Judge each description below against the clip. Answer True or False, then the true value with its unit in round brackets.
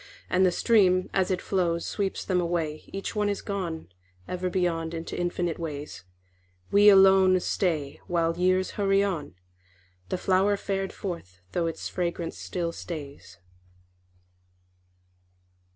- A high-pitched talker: False (180 Hz)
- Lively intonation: False (2.5 semitones)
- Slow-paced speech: True (130 wpm)